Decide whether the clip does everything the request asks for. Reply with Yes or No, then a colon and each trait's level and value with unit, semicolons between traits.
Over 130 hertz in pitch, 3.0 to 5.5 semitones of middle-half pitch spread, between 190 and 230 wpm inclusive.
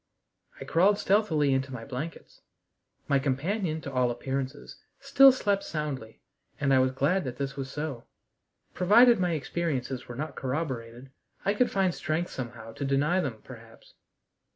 No: medium, 140 Hz; average, 5.0 semitones; average, 155 wpm